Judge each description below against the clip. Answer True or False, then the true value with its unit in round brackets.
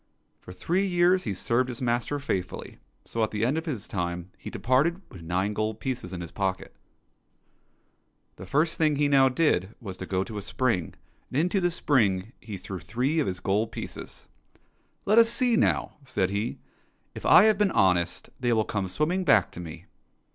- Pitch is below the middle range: True (115 Hz)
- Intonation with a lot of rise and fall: True (8.2 semitones)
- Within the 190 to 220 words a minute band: True (200 wpm)